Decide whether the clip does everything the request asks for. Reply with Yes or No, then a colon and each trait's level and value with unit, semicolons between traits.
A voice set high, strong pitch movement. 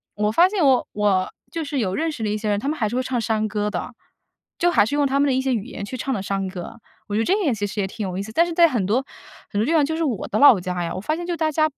Yes: high, 235 Hz; wide, 6.2 semitones